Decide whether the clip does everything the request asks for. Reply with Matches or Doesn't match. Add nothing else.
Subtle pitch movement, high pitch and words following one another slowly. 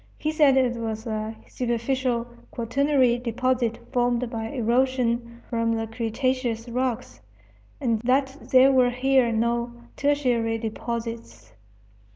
Matches